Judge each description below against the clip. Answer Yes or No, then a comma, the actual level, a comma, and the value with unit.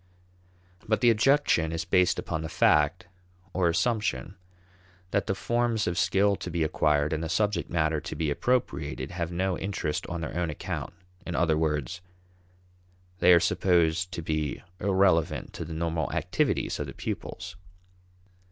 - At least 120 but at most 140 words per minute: No, average, 155 wpm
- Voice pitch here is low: Yes, very low, 85 Hz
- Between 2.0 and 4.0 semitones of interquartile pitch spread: Yes, average, 3.2 semitones